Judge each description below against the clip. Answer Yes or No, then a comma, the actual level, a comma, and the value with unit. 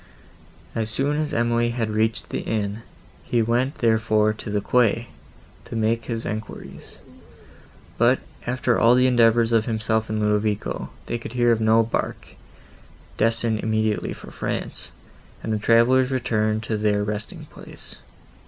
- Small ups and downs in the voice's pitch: Yes, narrow, 1.6 semitones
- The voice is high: No, low, 115 Hz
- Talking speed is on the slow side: No, average, 145 wpm